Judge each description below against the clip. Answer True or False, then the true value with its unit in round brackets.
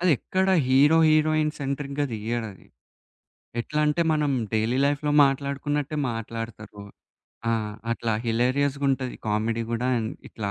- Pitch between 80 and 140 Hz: True (135 Hz)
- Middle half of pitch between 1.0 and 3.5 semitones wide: False (4.4 semitones)